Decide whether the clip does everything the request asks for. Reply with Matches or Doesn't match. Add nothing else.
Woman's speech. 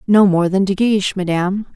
Matches